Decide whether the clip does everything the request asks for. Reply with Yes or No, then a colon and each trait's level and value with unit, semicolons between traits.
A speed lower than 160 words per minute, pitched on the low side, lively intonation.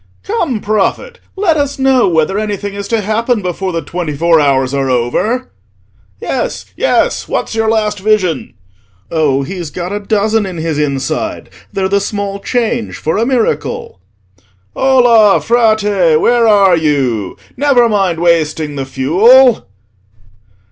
No: average, 140 wpm; high, 200 Hz; wide, 6.2 semitones